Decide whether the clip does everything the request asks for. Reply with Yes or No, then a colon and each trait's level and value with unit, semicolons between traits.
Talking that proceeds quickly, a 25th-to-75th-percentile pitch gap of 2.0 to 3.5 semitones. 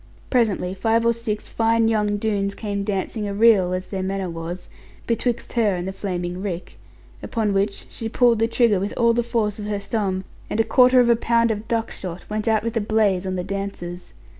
Yes: fast, 215 wpm; average, 3.0 semitones